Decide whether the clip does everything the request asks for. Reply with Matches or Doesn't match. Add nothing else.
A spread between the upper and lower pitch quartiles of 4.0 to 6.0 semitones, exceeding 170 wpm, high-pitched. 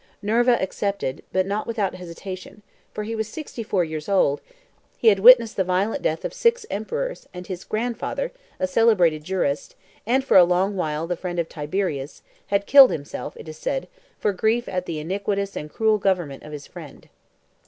Matches